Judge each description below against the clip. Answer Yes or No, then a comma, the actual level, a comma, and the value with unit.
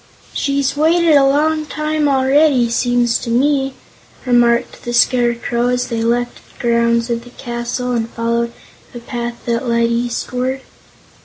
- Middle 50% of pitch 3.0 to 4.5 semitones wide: No, narrow, 2.5 semitones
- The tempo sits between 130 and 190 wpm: Yes, average, 145 wpm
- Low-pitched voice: No, high, 245 Hz